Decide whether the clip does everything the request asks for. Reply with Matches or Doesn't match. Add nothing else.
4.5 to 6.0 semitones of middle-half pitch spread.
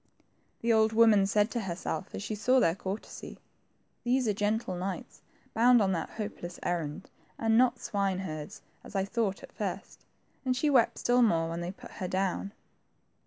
Doesn't match